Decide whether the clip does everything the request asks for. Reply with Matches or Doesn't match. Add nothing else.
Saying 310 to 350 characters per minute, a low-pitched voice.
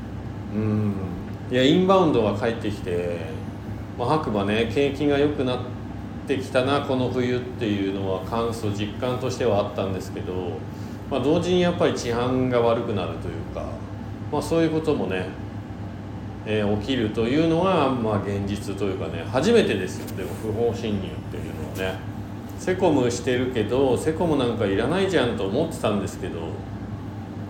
Matches